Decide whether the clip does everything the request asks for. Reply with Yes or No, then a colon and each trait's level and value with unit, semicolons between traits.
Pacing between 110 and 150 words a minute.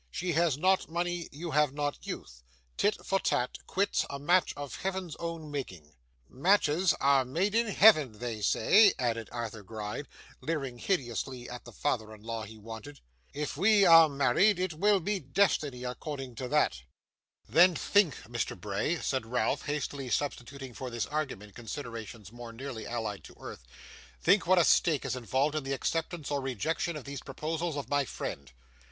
No: average, 170 wpm